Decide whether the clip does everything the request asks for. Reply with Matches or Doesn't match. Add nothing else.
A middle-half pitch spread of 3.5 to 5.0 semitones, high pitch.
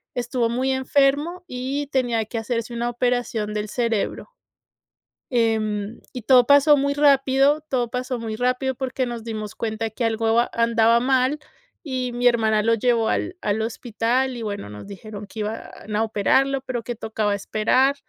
Doesn't match